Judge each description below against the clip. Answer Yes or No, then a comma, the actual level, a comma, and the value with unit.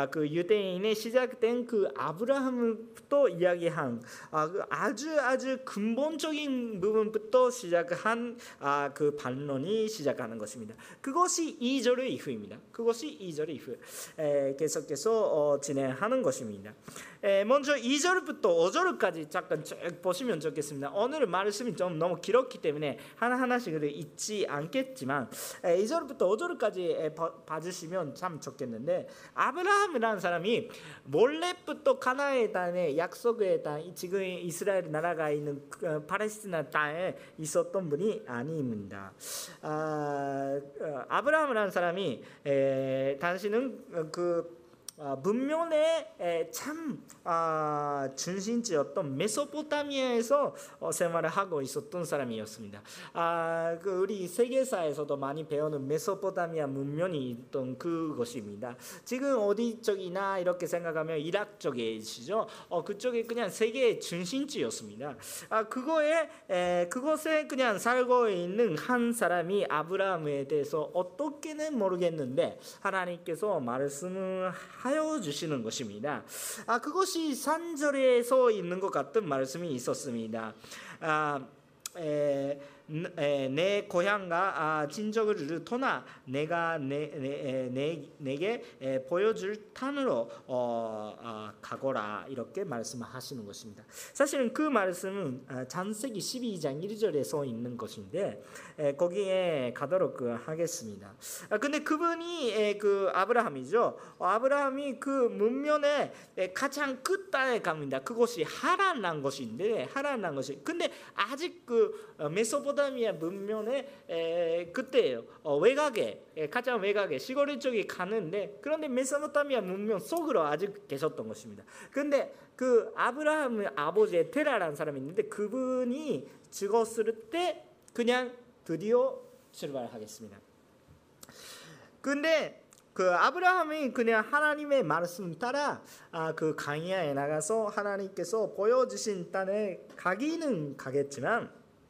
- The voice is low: No, high, 200 Hz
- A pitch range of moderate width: No, wide, 9.0 semitones